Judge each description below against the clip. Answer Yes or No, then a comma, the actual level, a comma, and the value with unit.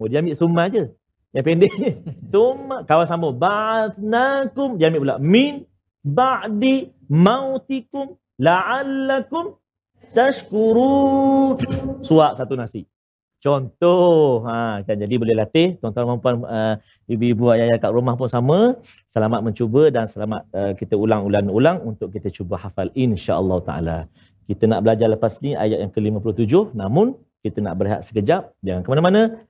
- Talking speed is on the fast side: Yes, fast, 135 wpm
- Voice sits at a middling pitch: No, low, 130 Hz